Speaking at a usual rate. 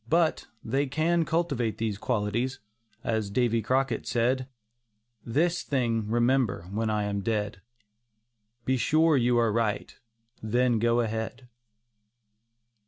No: slow, 115 wpm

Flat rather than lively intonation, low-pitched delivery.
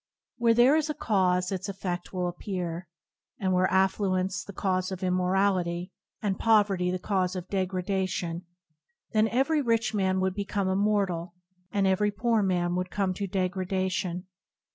No: narrow, 1.9 semitones; high, 190 Hz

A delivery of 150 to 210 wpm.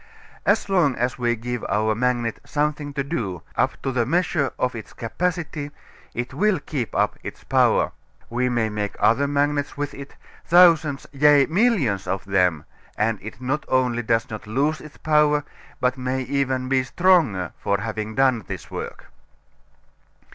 Yes: average, 160 wpm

